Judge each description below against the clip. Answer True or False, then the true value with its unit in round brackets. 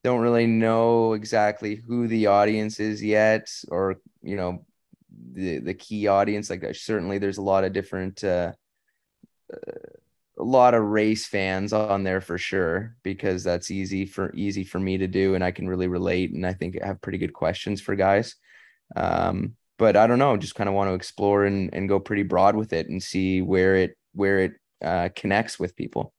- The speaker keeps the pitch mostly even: True (2.3 semitones)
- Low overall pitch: True (100 Hz)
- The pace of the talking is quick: False (195 wpm)